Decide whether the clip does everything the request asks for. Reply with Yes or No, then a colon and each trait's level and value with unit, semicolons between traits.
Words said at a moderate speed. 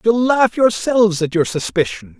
Yes: average, 165 wpm